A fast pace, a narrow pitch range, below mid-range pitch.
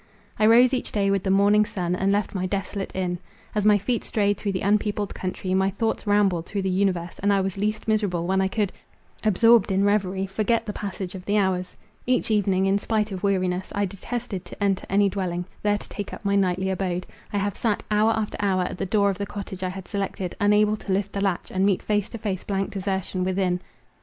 No: fast, 225 wpm; narrow, 1.7 semitones; high, 200 Hz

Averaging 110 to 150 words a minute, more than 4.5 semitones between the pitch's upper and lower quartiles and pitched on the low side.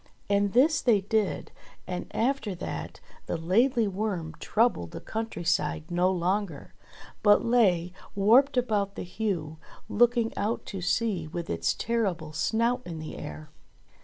No: average, 140 wpm; average, 5.0 semitones; high, 200 Hz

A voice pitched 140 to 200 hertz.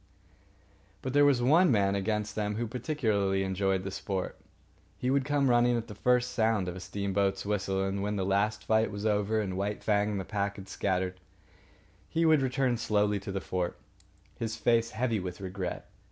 No: low, 105 Hz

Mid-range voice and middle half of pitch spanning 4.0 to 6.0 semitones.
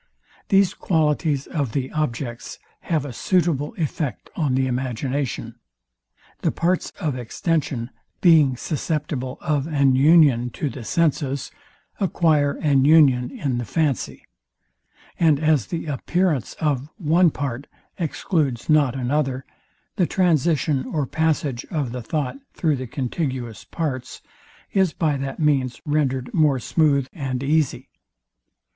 No: medium, 145 Hz; average, 3.6 semitones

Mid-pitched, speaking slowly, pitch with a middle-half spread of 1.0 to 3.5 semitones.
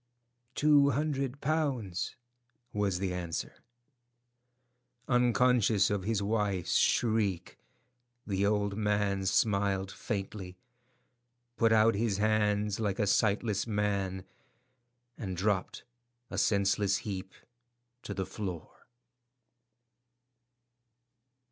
No: low, 105 Hz; slow, 90 wpm; narrow, 2.5 semitones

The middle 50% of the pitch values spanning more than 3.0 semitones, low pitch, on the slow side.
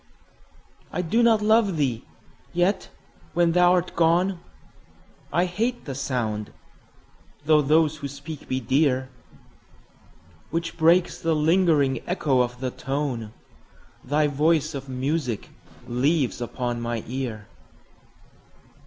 No: average, 4.8 semitones; medium, 150 Hz; slow, 115 wpm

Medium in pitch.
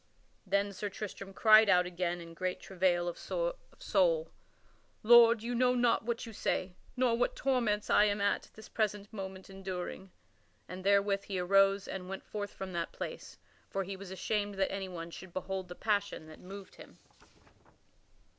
No: high, 195 Hz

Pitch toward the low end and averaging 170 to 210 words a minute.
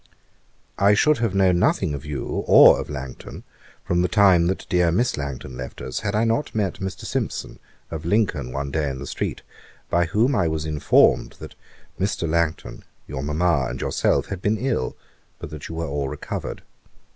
Yes: very low, 85 Hz; average, 190 wpm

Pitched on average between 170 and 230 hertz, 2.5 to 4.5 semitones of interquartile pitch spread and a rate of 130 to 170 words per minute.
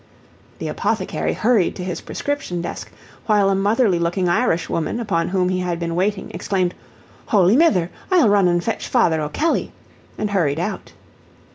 Yes: medium, 185 Hz; average, 3.6 semitones; average, 160 wpm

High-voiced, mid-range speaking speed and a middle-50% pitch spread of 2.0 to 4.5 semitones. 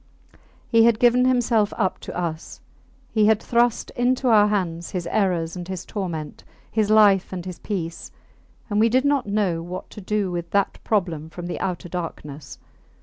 Yes: high, 195 Hz; average, 175 wpm; average, 4.1 semitones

